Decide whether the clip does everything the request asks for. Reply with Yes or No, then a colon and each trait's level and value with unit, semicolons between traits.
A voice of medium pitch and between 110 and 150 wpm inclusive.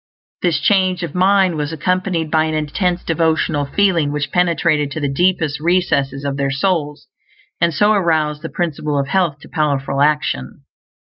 No: medium, 160 Hz; average, 160 wpm